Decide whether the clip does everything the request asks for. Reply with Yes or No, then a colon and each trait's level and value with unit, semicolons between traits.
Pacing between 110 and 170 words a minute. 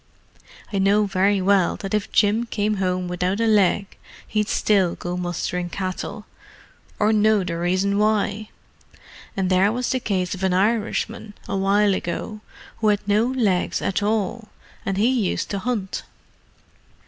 Yes: average, 150 wpm